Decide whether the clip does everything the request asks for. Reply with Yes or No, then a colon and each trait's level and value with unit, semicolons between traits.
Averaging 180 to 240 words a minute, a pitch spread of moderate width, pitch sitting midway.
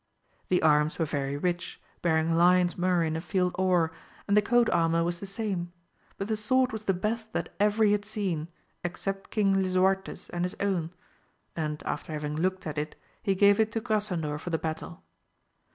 Yes: average, 190 wpm; average, 3.8 semitones; medium, 180 Hz